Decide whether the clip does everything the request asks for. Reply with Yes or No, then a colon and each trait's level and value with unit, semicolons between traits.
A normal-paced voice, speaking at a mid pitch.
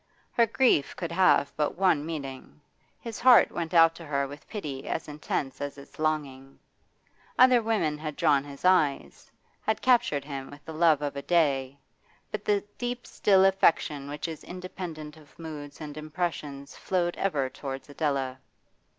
Yes: average, 160 wpm; medium, 155 Hz